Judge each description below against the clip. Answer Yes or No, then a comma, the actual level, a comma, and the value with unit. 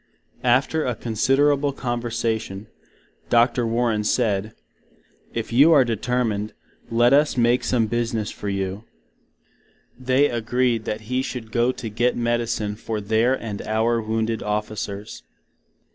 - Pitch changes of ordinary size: No, narrow, 2.3 semitones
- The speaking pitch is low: Yes, low, 115 Hz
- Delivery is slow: Yes, slow, 125 wpm